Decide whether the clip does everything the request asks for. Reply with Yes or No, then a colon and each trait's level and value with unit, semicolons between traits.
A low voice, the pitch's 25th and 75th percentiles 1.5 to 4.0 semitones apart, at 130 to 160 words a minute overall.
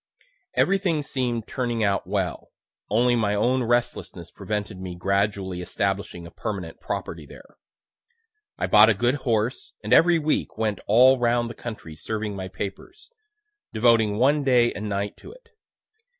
Yes: low, 110 Hz; average, 3.7 semitones; average, 150 wpm